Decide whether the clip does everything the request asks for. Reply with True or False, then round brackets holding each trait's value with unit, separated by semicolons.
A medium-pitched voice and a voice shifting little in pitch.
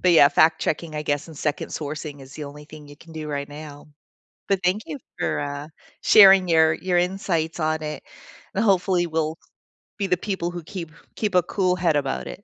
False (160 Hz; 3.3 semitones)